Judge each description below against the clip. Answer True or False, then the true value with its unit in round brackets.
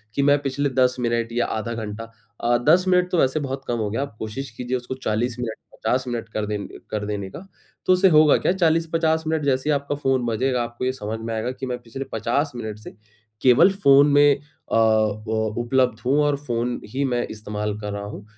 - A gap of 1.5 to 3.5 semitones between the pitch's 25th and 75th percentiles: False (4.2 semitones)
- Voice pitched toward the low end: True (125 Hz)